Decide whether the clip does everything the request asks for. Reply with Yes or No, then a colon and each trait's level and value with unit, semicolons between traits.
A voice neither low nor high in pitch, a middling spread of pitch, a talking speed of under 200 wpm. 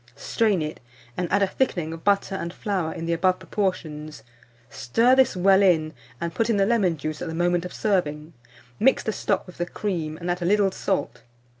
No: medium, 180 Hz; average, 3.7 semitones; fast, 205 wpm